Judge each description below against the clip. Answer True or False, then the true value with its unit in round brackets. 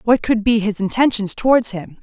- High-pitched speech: True (220 Hz)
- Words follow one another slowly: False (205 wpm)